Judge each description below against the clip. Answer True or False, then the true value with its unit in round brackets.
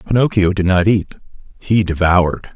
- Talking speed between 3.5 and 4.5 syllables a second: False (5.3 syllables/s)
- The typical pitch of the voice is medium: False (95 Hz)